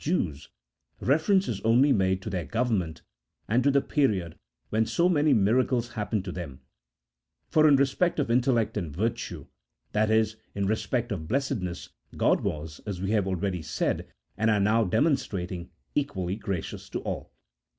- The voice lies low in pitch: Yes, low, 110 Hz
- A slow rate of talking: No, average, 175 wpm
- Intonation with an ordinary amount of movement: No, wide, 6.1 semitones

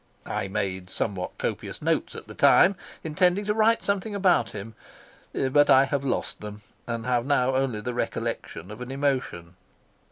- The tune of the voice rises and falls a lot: Yes, wide, 6.2 semitones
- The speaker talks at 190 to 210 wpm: No, average, 165 wpm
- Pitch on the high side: No, low, 130 Hz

